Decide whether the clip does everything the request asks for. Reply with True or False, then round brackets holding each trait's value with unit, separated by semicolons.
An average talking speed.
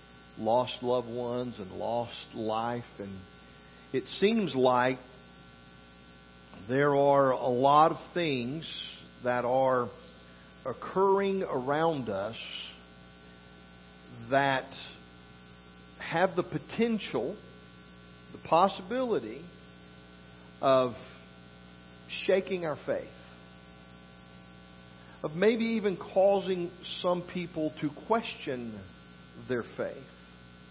False (80 wpm)